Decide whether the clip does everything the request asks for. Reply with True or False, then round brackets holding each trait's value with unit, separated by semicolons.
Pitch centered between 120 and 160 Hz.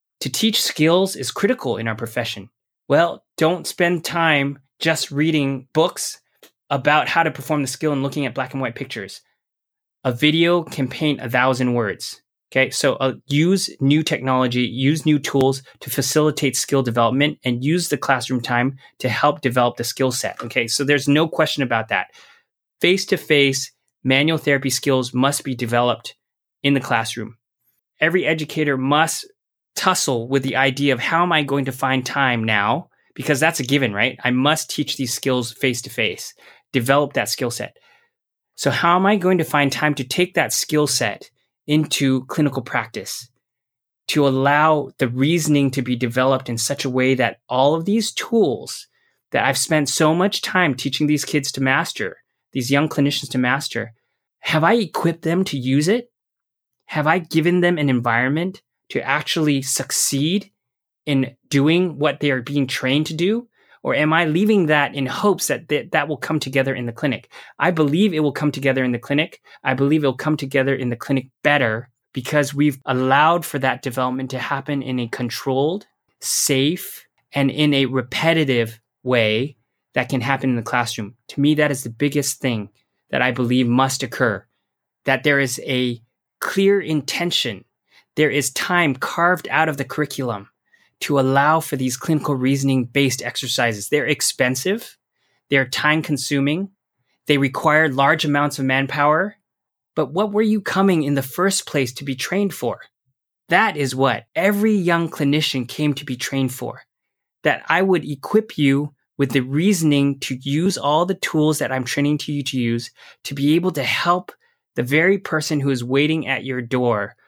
True (140 Hz)